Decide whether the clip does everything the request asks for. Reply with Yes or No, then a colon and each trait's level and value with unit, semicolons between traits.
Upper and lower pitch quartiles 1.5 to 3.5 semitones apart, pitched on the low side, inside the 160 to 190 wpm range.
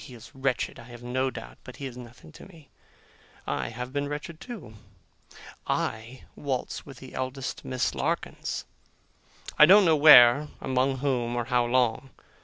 Yes: average, 2.7 semitones; low, 130 Hz; average, 165 wpm